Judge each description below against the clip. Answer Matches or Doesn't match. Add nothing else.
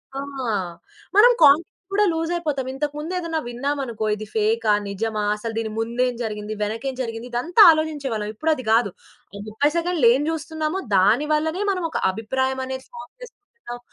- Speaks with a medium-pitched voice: Doesn't match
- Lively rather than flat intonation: Matches